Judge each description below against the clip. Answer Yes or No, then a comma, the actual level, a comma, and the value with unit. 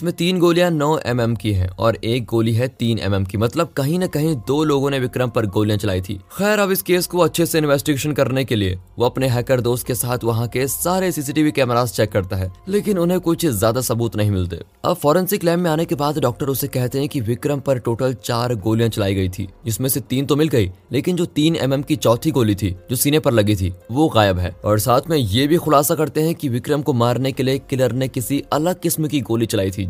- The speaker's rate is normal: No, fast, 255 wpm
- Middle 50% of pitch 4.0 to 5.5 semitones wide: Yes, average, 5.2 semitones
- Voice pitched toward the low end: Yes, low, 130 Hz